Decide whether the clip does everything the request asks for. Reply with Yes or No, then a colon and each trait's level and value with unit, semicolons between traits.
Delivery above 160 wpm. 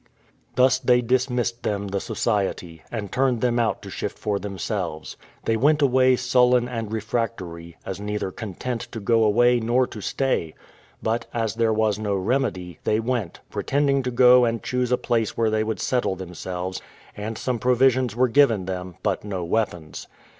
Yes: average, 170 wpm